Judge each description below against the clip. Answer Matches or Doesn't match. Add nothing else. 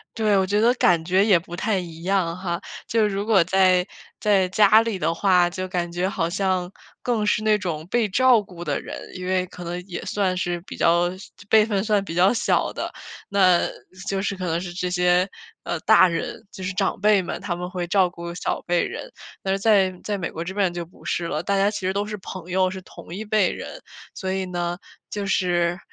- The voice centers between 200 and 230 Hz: Doesn't match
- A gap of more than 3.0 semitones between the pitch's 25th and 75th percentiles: Doesn't match